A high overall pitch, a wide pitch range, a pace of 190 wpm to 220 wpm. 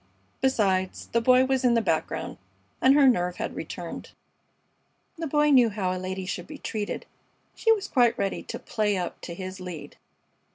No: high, 220 Hz; wide, 6.0 semitones; average, 175 wpm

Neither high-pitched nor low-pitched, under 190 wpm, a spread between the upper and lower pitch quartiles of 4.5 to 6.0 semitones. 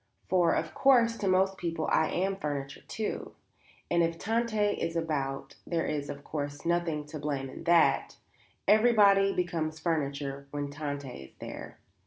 Yes: medium, 165 Hz; average, 155 wpm; average, 5.0 semitones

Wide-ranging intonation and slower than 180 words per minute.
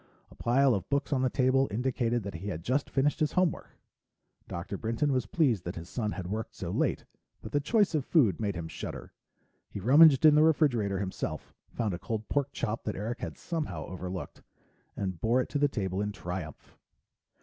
No: wide, 6.4 semitones; average, 200 wpm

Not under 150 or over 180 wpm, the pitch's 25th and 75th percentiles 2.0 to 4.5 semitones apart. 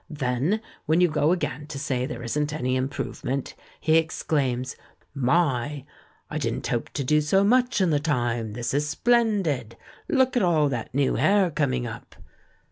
No: average, 165 wpm; average, 4.9 semitones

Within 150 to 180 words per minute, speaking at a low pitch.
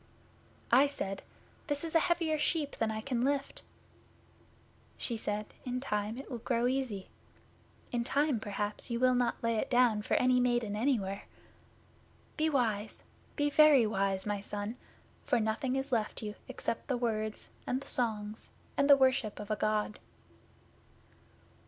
No: average, 155 wpm; high, 240 Hz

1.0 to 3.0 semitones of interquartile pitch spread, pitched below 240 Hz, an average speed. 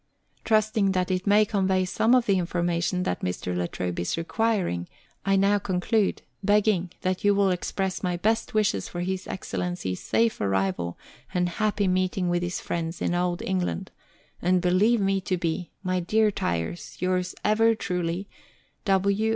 Yes: narrow, 2.6 semitones; medium, 185 Hz; average, 160 wpm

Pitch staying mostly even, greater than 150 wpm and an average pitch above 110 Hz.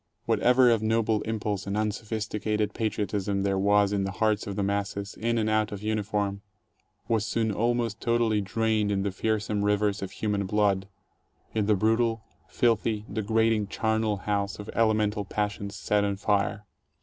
No: narrow, 1.5 semitones; average, 160 wpm; low, 105 Hz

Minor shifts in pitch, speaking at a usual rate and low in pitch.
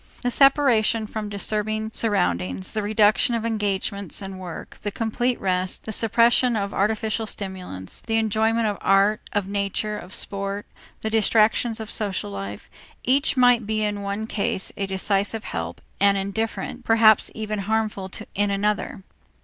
No: narrow, 2.0 semitones; average, 150 wpm; high, 210 Hz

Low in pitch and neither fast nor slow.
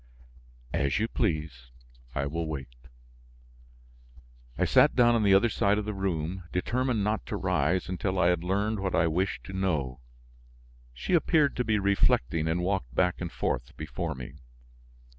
Yes: very low, 90 Hz; average, 160 wpm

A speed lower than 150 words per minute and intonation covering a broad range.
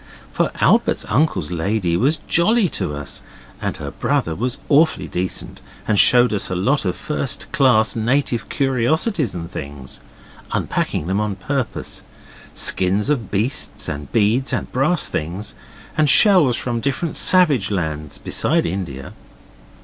Yes: average, 140 wpm; wide, 7.4 semitones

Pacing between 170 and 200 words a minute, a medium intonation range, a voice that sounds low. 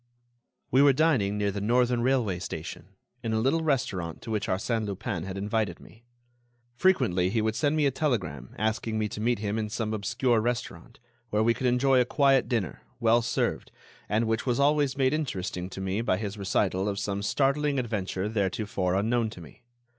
Yes: average, 190 wpm; average, 4.2 semitones; low, 110 Hz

